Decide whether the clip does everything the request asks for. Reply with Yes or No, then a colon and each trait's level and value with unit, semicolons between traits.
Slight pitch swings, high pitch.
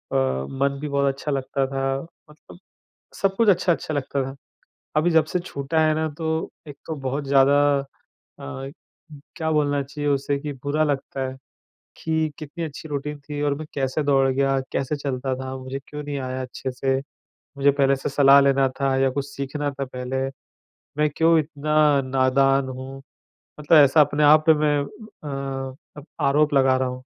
No: narrow, 1.9 semitones; medium, 140 Hz